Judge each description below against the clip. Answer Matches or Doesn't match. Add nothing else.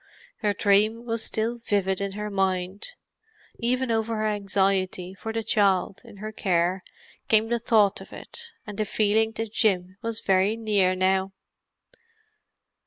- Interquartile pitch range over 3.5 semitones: Doesn't match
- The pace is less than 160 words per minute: Matches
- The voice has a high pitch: Matches